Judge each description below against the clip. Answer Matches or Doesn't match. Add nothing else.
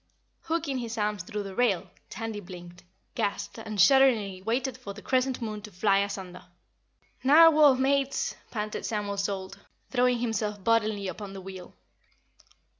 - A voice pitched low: Doesn't match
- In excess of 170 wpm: Doesn't match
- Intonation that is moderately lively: Matches